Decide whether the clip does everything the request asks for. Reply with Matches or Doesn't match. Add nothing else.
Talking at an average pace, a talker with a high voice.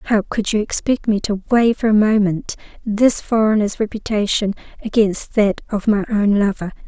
Matches